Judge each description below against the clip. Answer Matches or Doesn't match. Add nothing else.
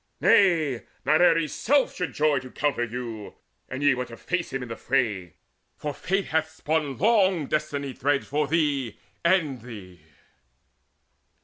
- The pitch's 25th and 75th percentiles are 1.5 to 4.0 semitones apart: Doesn't match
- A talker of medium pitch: Matches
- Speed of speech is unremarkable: Matches